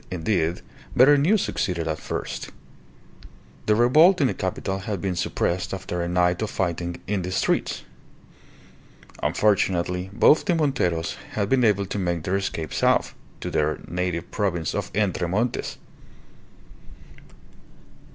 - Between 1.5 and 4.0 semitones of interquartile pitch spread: Yes, average, 3.6 semitones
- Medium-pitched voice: No, very low, 95 Hz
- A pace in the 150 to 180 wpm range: No, slow, 135 wpm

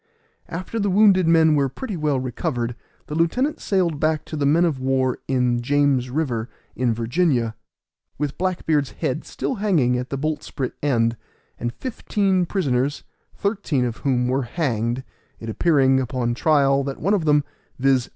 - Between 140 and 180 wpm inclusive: Yes, average, 160 wpm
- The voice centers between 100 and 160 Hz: Yes, medium, 140 Hz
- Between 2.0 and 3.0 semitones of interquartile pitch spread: No, average, 4.8 semitones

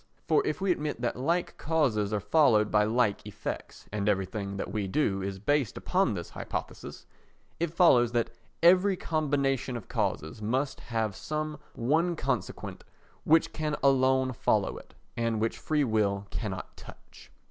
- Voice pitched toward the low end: Yes, low, 125 Hz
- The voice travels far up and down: Yes, wide, 6.4 semitones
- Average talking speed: Yes, average, 155 wpm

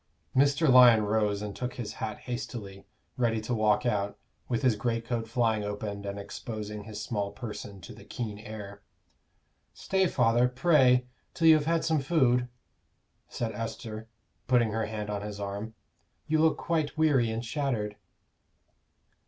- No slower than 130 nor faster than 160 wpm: Yes, average, 155 wpm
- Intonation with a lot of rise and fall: No, average, 3.2 semitones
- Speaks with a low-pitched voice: Yes, low, 115 Hz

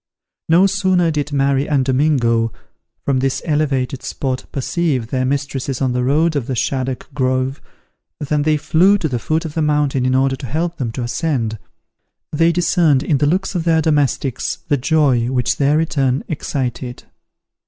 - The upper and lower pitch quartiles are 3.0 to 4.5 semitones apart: Yes, average, 3.4 semitones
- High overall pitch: No, medium, 140 Hz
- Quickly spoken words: No, average, 170 wpm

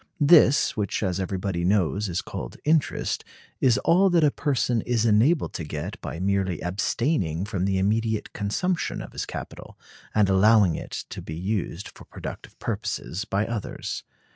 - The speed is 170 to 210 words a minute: No, average, 160 wpm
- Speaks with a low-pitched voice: Yes, low, 105 Hz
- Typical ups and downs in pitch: Yes, average, 4.3 semitones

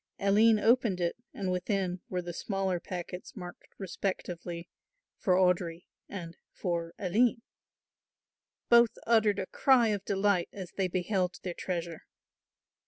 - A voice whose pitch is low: No, medium, 185 Hz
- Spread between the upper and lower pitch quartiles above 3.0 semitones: No, narrow, 2.6 semitones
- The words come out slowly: Yes, slow, 125 wpm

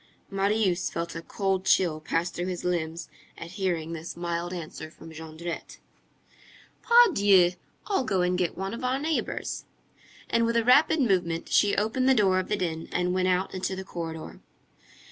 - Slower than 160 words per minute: No, average, 170 wpm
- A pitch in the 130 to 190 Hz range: Yes, medium, 185 Hz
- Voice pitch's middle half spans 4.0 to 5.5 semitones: No, average, 3.5 semitones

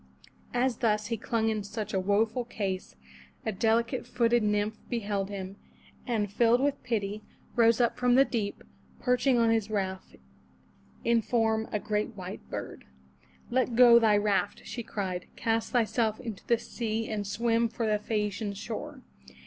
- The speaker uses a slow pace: No, average, 165 wpm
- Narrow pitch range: Yes, narrow, 2.3 semitones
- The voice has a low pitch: No, high, 225 Hz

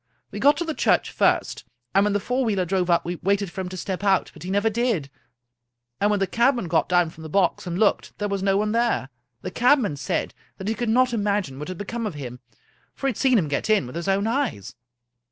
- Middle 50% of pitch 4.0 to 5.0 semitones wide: Yes, average, 4.4 semitones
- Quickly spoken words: Yes, fast, 250 wpm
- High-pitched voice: Yes, high, 200 Hz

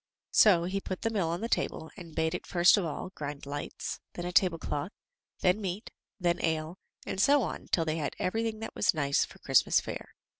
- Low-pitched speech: No, medium, 175 Hz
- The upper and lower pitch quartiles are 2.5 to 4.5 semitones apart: Yes, average, 3.6 semitones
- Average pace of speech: No, fast, 210 wpm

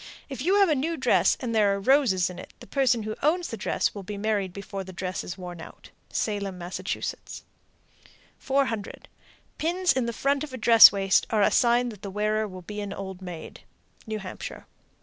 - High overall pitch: Yes, high, 215 Hz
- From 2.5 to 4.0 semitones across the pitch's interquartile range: No, average, 5.1 semitones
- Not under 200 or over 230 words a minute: Yes, fast, 205 wpm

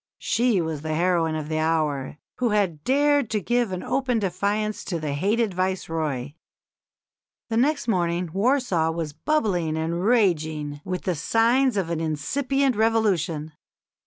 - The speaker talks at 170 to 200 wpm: No, average, 140 wpm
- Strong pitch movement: Yes, wide, 6.2 semitones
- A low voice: No, medium, 185 Hz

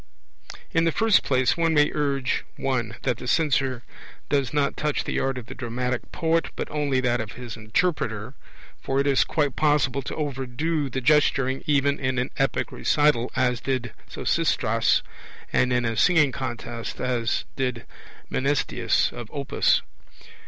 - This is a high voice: No, low, 135 Hz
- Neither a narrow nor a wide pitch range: Yes, average, 3.0 semitones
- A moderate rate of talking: Yes, average, 155 wpm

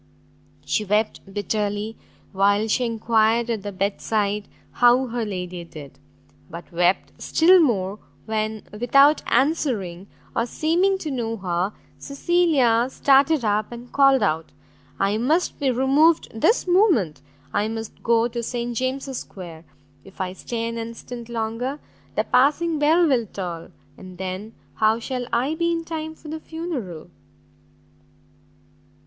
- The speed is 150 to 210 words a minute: No, average, 140 wpm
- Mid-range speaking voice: No, high, 230 Hz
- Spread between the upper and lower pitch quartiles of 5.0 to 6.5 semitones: Yes, wide, 5.4 semitones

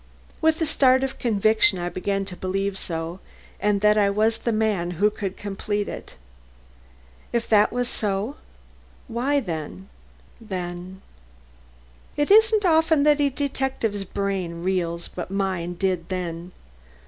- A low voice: No, high, 200 Hz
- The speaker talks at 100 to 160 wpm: Yes, slow, 135 wpm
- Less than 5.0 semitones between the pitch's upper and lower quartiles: No, average, 5.3 semitones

